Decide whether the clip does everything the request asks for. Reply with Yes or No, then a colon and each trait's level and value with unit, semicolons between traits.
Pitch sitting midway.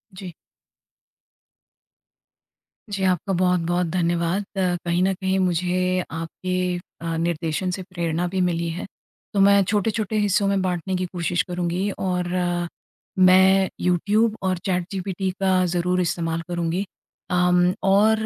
Yes: medium, 180 Hz